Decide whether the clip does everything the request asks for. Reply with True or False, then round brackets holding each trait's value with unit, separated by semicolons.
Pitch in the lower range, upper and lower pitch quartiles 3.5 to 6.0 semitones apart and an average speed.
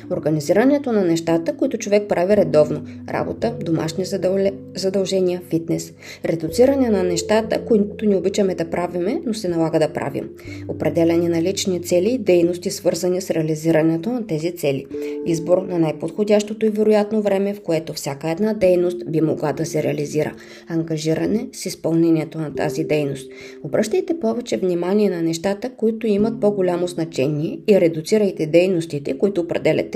False (175 Hz; 4.5 semitones; 145 wpm)